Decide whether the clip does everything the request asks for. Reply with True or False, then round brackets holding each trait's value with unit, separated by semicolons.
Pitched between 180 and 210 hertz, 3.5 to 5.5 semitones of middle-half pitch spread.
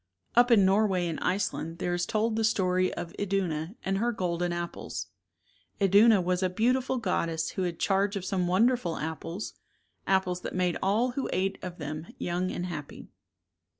False (185 Hz; 2.9 semitones)